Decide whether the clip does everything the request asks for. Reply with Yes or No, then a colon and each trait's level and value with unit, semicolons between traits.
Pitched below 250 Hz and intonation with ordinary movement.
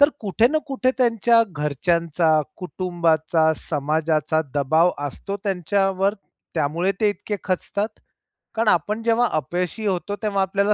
Yes: medium, 185 Hz; average, 4.7 semitones